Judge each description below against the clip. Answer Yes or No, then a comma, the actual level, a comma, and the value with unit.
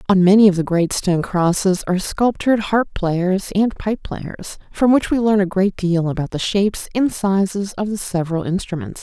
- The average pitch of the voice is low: No, high, 190 Hz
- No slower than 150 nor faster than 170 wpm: No, average, 200 wpm